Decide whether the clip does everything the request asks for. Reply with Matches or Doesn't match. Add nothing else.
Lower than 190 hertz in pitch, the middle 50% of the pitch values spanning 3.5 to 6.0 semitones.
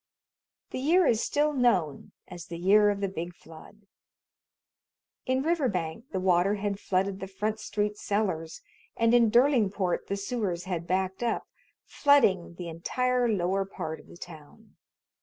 Doesn't match